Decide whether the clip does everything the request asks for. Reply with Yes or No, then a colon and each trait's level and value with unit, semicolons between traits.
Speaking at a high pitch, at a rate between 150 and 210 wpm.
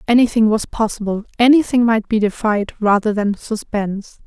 No: high, 220 Hz; average, 140 wpm